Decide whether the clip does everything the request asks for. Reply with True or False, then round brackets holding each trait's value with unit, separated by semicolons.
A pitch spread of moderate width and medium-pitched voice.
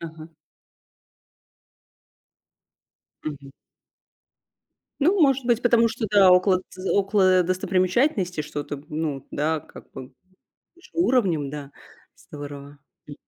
False (6.8 semitones; 180 Hz)